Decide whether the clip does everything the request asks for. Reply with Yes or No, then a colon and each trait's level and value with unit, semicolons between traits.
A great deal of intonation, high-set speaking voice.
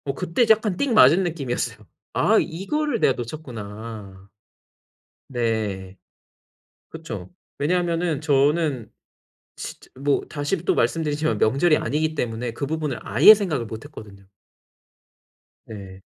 No: wide, 6.6 semitones; medium, 140 Hz